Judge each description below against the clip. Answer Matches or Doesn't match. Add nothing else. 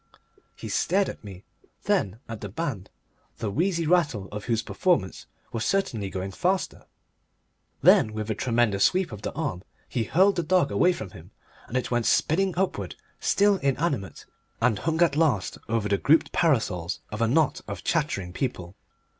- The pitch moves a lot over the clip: Matches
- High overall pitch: Doesn't match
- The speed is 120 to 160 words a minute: Doesn't match